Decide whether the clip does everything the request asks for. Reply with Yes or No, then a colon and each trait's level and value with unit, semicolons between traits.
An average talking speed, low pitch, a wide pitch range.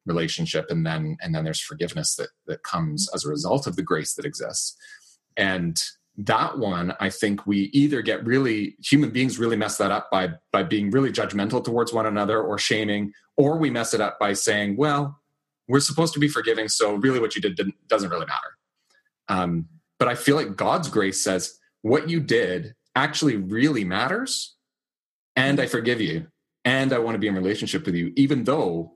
Yes: average, 195 wpm; low, 115 Hz; wide, 6.3 semitones